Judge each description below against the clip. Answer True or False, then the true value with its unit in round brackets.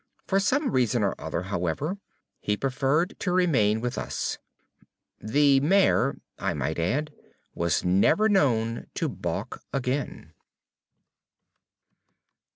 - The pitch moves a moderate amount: False (8.0 semitones)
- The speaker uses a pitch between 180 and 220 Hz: False (135 Hz)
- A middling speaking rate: False (110 wpm)